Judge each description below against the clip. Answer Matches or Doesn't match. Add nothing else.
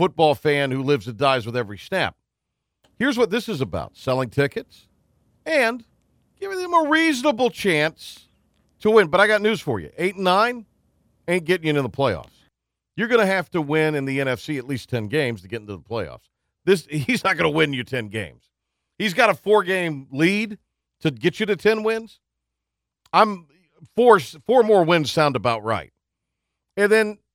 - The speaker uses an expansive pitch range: Matches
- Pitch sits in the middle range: Matches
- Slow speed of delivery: Doesn't match